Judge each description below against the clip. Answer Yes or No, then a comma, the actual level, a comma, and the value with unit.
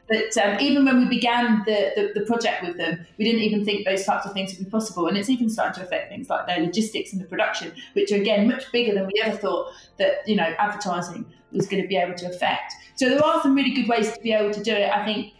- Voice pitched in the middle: No, high, 210 Hz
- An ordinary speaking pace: No, fast, 275 wpm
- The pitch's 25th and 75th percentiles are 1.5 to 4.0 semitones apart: Yes, average, 3.3 semitones